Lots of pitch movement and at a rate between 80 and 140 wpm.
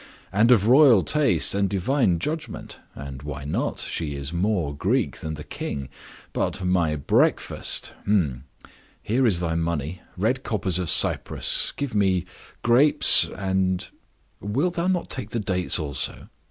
Yes: wide, 6.3 semitones; slow, 135 wpm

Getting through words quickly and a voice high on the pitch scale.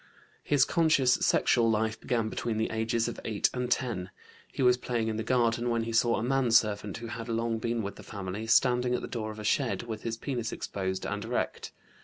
No: fast, 215 wpm; low, 115 Hz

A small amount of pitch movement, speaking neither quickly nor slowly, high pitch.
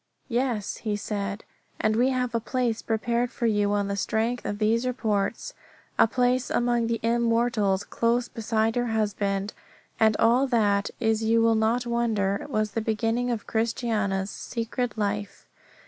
Yes: narrow, 2.2 semitones; average, 155 wpm; high, 225 Hz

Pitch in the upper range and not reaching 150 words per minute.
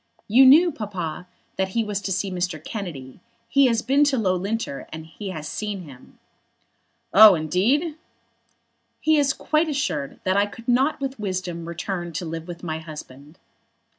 No: high, 195 Hz; average, 160 wpm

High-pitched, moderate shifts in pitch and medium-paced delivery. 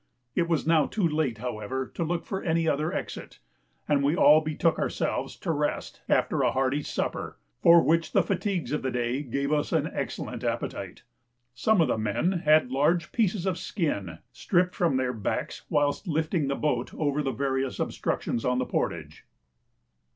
No: medium, 150 Hz; average, 4.3 semitones; average, 180 wpm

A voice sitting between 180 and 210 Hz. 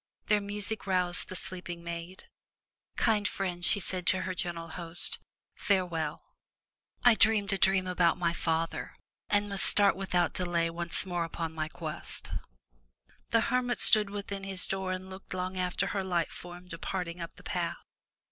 Yes: medium, 185 Hz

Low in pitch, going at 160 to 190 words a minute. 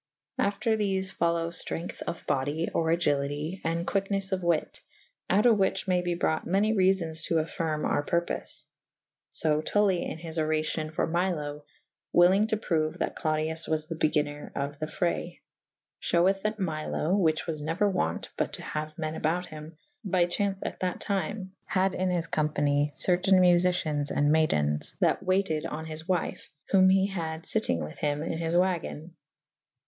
No: medium, 165 Hz; average, 175 wpm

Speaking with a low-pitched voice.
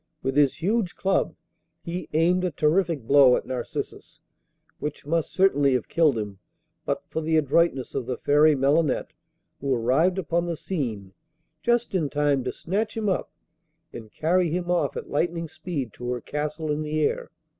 No: medium, 155 Hz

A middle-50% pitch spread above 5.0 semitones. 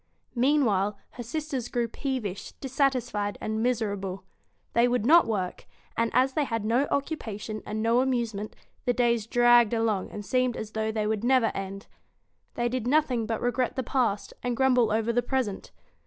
No: average, 3.0 semitones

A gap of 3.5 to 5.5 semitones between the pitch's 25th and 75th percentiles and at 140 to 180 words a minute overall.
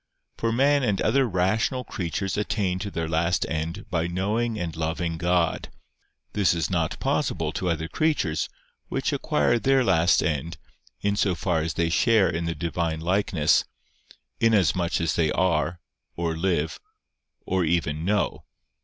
Yes: average, 3.9 semitones; average, 150 wpm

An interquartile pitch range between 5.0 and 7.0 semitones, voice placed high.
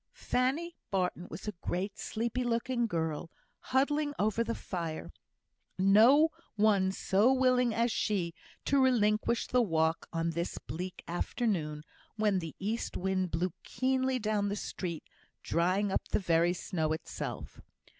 Yes: wide, 5.6 semitones; high, 205 Hz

